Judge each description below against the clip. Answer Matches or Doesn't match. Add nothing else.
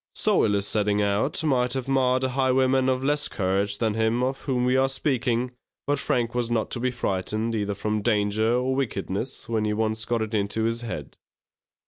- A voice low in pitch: Matches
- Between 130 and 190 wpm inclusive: Doesn't match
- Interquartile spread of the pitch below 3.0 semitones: Doesn't match